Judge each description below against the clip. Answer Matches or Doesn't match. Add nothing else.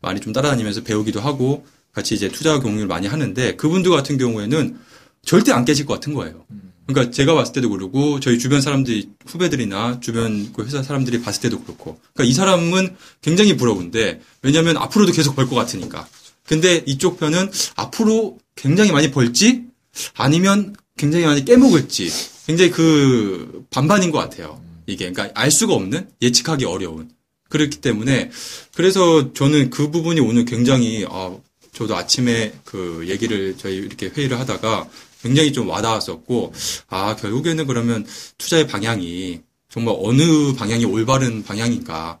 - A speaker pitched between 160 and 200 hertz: Doesn't match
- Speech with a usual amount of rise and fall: Doesn't match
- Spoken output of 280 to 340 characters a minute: Doesn't match